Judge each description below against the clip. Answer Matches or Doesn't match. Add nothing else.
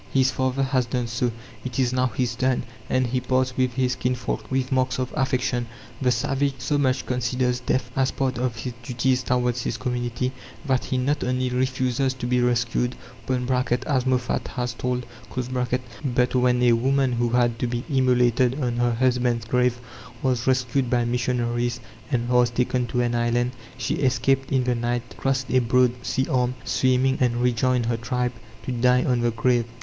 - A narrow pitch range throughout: Matches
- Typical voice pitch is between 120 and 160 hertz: Matches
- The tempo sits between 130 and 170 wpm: Doesn't match